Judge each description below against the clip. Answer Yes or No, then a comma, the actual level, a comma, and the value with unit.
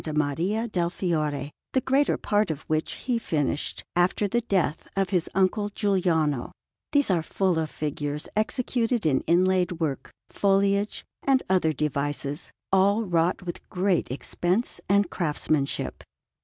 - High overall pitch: No, medium, 180 Hz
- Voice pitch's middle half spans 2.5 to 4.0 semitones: No, average, 4.7 semitones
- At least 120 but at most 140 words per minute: Yes, slow, 135 wpm